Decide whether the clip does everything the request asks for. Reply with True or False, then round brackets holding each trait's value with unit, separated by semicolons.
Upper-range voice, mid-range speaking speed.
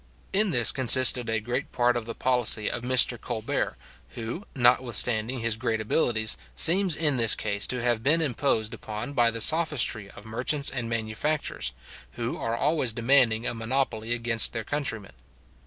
False (120 Hz; 160 wpm)